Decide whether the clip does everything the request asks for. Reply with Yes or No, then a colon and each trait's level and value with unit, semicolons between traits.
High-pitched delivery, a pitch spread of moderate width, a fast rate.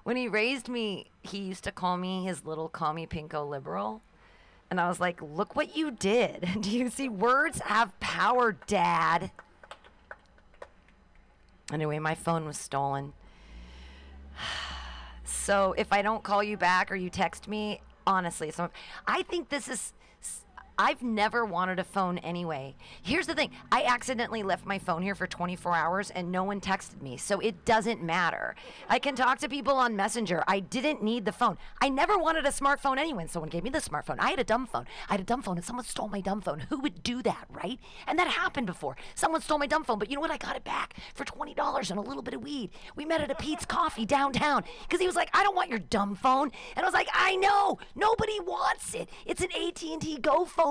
No: high, 215 Hz; wide, 8.0 semitones; fast, 210 wpm